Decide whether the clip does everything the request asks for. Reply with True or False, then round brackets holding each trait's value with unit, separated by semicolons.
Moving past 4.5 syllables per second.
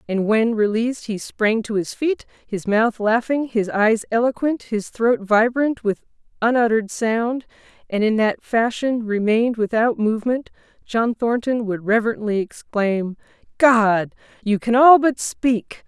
False (4.2 syllables/s)